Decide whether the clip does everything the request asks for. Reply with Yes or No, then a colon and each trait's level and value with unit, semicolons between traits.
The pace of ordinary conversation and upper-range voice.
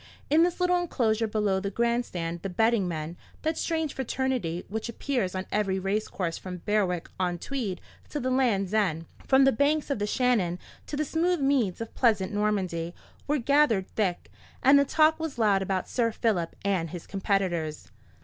Yes: average, 170 wpm; high, 215 Hz